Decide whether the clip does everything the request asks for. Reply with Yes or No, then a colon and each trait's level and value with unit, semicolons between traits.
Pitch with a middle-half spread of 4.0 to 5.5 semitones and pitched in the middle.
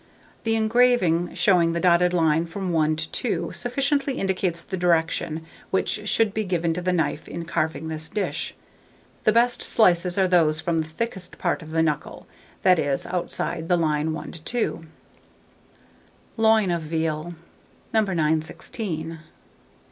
No: average, 3.6 semitones; medium, 175 Hz